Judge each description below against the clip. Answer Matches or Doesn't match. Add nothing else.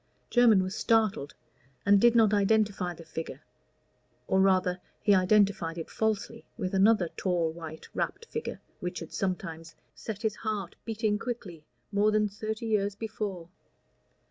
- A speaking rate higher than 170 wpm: Doesn't match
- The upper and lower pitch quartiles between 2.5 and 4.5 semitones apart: Matches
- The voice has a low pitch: Doesn't match